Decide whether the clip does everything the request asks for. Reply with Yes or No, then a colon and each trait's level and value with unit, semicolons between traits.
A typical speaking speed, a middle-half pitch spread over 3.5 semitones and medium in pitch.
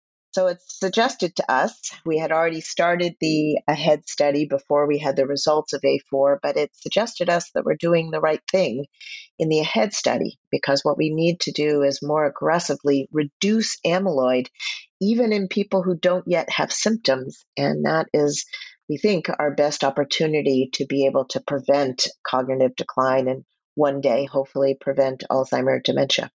Yes: average, 170 wpm; average, 3.9 semitones; medium, 150 Hz